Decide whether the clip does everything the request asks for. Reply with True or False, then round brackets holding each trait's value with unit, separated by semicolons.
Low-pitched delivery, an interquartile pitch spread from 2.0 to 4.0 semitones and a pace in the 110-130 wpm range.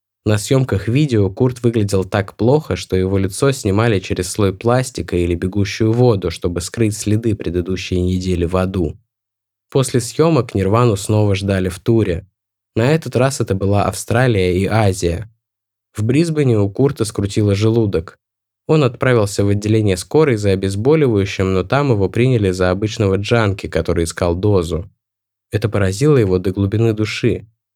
False (105 Hz; 3.6 semitones; 145 wpm)